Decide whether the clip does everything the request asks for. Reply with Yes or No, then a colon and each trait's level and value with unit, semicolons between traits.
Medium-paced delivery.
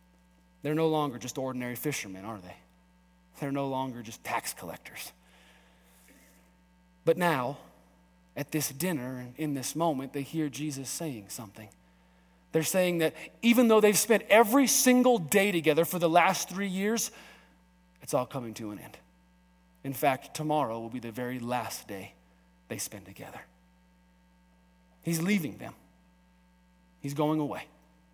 Yes: average, 145 wpm